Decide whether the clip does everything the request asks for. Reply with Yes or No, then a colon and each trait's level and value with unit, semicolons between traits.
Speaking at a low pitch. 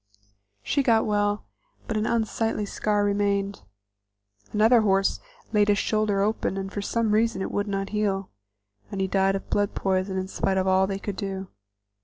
No: high, 205 Hz